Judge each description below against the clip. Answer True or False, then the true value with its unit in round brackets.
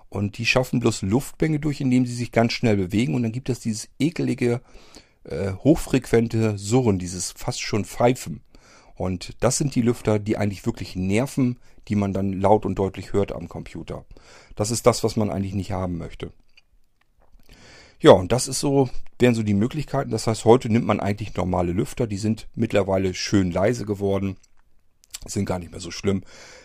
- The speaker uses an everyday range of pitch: True (3.8 semitones)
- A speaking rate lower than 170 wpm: False (180 wpm)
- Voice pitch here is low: True (110 Hz)